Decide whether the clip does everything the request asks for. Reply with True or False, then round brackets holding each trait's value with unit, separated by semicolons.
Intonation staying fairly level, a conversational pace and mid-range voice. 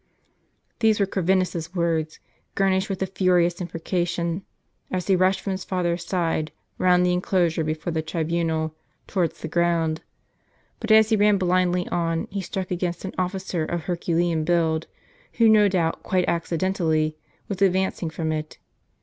True (2.3 semitones; 150 wpm; 175 Hz)